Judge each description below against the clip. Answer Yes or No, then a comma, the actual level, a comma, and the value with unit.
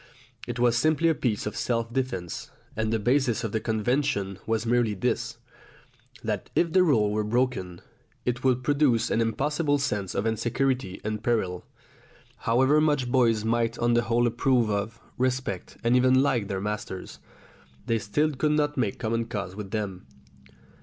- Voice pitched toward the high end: No, low, 115 Hz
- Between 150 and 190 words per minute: Yes, average, 165 wpm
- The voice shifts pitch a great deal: No, average, 3.5 semitones